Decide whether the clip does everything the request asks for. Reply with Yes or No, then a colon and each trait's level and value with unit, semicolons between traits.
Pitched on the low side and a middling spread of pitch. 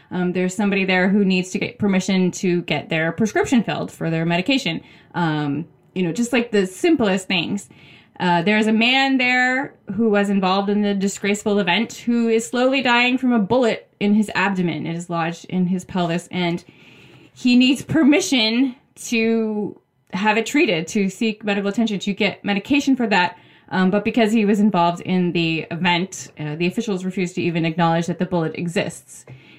No: high, 200 Hz; average, 4.4 semitones